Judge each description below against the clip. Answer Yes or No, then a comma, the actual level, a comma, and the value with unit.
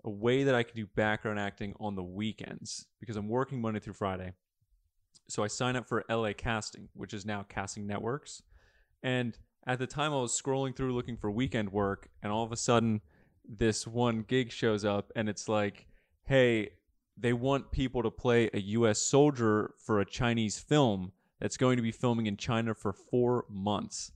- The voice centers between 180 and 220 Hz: No, low, 110 Hz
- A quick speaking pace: No, average, 190 wpm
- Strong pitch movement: No, average, 3.0 semitones